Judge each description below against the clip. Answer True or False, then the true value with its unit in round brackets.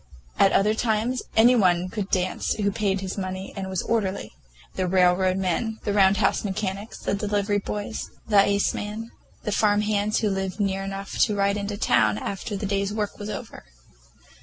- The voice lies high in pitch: True (200 Hz)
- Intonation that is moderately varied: False (1.7 semitones)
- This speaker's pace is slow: False (175 wpm)